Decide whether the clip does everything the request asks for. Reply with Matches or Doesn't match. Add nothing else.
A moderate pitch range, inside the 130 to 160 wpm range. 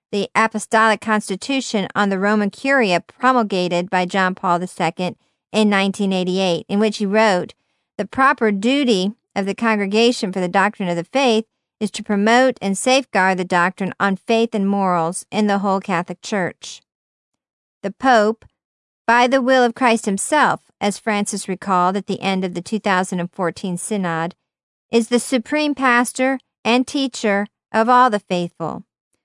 Matches